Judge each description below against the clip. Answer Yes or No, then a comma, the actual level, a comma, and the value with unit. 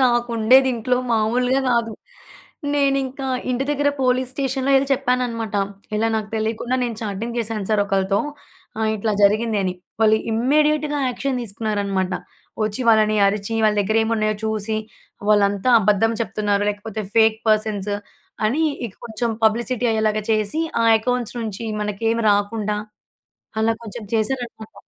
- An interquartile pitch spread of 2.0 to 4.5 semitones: Yes, average, 2.8 semitones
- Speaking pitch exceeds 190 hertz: Yes, high, 220 Hz